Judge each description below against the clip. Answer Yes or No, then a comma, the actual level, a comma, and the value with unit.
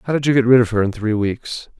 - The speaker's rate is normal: No, fast, 335 wpm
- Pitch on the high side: No, low, 115 Hz